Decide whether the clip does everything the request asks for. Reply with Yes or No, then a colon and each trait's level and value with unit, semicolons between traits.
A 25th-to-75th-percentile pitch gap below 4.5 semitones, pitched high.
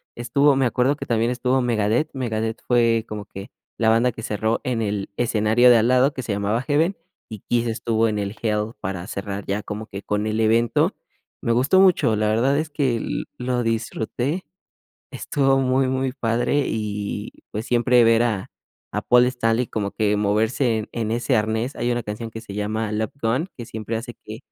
No: narrow, 2.6 semitones; low, 115 Hz